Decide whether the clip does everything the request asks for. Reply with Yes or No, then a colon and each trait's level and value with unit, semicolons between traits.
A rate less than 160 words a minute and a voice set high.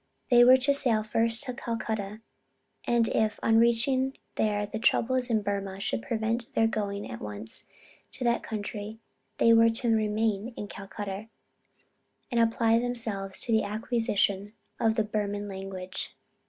Yes: average, 150 wpm; high, 220 Hz